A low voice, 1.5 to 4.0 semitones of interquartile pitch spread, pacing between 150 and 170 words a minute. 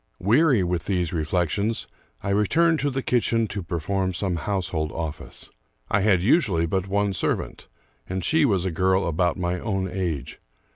Yes: very low, 95 Hz; average, 3.3 semitones; average, 165 wpm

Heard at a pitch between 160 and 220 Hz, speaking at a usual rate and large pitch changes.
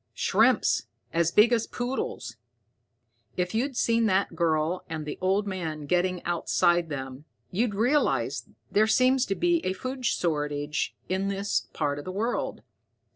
Yes: medium, 185 Hz; average, 150 wpm; wide, 6.0 semitones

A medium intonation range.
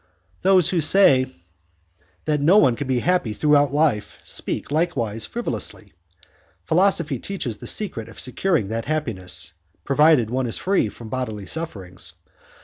No: wide, 6.5 semitones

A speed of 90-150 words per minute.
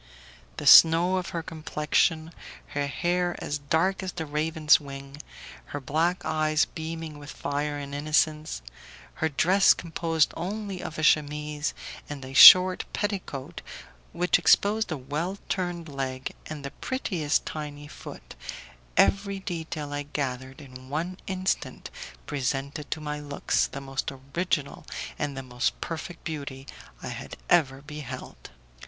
Yes: slow, 135 wpm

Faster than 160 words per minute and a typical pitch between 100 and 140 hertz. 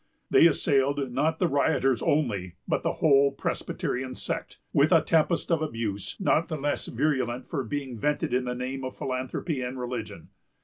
Yes: average, 170 wpm; low, 135 Hz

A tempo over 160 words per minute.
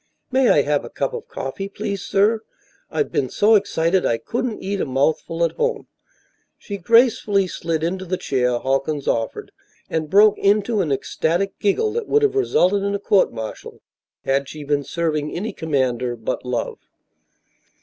Yes: average, 170 wpm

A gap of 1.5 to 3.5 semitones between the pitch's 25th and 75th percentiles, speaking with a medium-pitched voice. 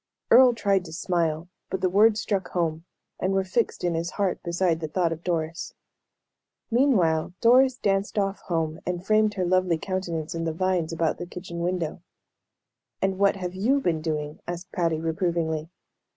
Yes: average, 2.9 semitones; medium, 180 Hz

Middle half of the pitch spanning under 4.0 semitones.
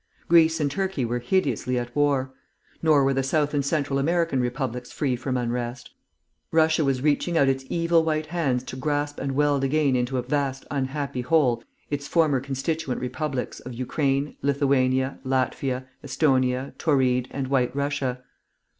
Yes: narrow, 2.6 semitones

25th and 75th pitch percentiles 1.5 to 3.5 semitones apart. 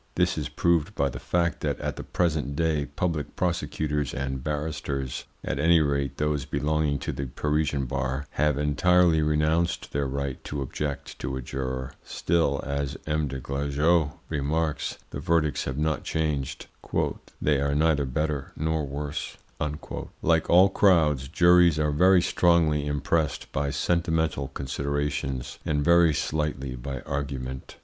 Yes: narrow, 2.4 semitones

